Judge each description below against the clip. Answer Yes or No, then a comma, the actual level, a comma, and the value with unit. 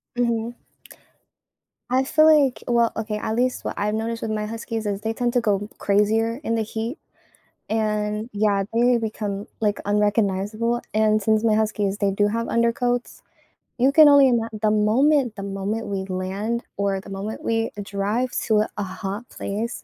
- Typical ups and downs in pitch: No, narrow, 2.2 semitones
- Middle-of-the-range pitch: No, high, 220 Hz